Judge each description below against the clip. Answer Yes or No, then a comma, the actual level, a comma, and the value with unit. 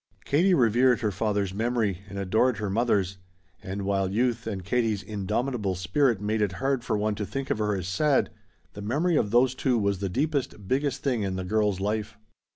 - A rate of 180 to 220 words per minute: Yes, average, 195 wpm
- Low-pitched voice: Yes, low, 105 Hz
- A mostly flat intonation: No, average, 3.9 semitones